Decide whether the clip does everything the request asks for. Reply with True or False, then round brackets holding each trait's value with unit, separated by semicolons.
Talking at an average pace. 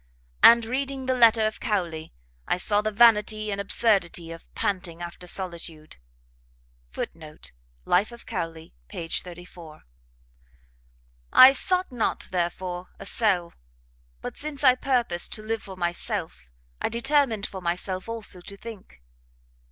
False (130 wpm)